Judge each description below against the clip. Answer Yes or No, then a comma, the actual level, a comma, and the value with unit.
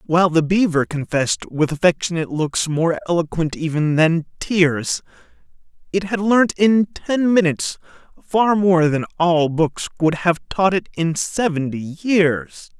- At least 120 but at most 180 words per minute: Yes, average, 140 wpm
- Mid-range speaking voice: Yes, medium, 170 Hz